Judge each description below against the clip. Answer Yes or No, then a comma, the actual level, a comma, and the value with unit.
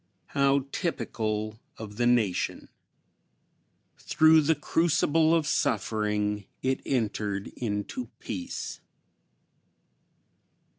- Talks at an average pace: No, slow, 80 wpm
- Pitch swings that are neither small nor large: No, wide, 5.9 semitones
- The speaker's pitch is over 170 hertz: No, low, 120 Hz